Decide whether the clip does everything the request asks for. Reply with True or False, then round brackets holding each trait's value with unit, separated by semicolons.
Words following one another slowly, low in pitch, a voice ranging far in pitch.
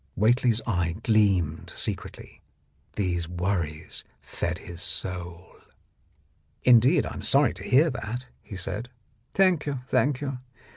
True (125 wpm; 105 Hz; 6.3 semitones)